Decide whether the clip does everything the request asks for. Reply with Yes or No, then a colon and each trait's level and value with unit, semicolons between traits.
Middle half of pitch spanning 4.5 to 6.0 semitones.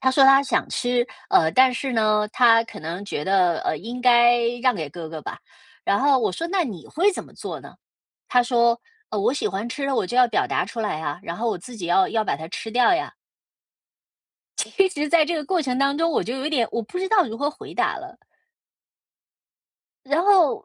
Yes: average, 5.2 semitones